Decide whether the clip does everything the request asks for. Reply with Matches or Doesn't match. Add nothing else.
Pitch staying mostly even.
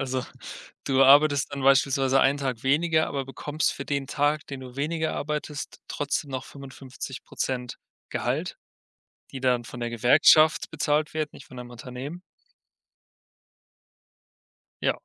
Matches